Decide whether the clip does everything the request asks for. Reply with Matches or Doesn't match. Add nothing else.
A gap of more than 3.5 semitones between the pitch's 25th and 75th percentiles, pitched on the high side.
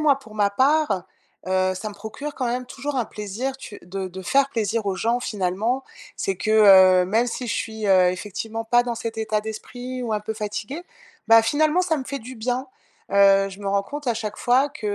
Matches